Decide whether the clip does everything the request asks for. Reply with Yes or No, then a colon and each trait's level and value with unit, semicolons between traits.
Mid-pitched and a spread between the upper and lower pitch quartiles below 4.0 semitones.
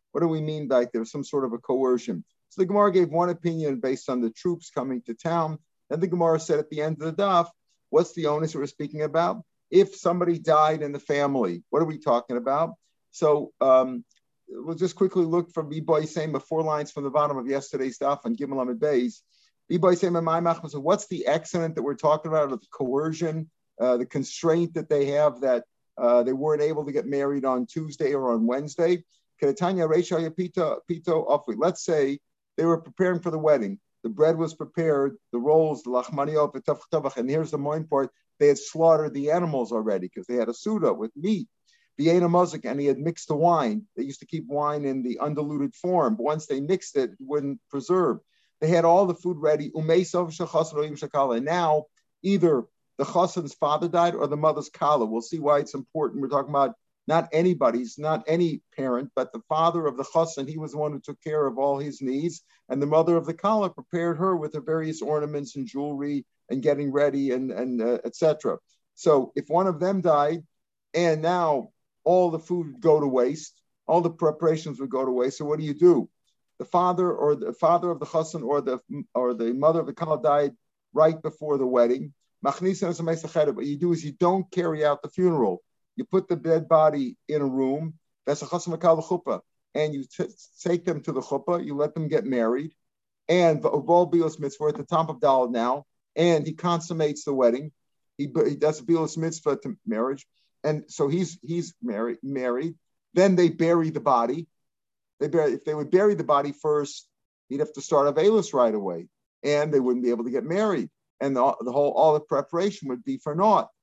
Yes: medium, 155 Hz; average, 3.4 semitones